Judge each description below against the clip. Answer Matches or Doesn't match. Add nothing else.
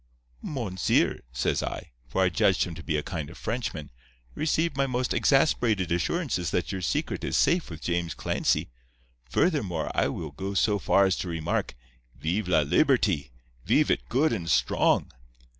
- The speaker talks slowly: Doesn't match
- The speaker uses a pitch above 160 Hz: Doesn't match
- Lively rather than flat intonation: Matches